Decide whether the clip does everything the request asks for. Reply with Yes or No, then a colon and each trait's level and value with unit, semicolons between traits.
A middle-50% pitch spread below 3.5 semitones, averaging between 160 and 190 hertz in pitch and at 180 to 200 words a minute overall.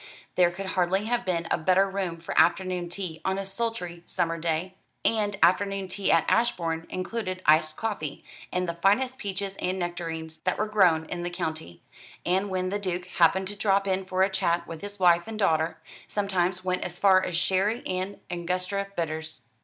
Yes: narrow, 2.6 semitones; medium, 185 Hz; average, 185 wpm